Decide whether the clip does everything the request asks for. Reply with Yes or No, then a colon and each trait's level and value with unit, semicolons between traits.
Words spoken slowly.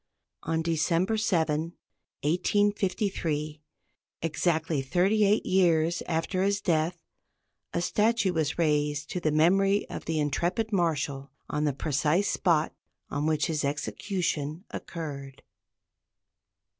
Yes: slow, 110 wpm